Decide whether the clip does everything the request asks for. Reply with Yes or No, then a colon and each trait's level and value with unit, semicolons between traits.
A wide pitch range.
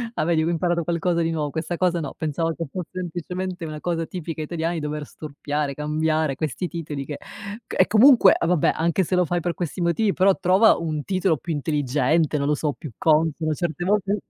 No: average, 2.7 semitones